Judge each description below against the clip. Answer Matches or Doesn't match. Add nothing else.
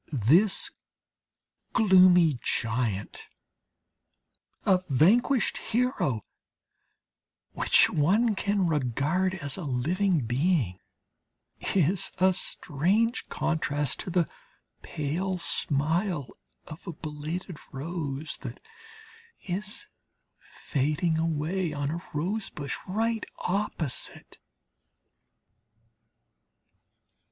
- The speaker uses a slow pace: Matches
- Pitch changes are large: Doesn't match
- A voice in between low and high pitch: Matches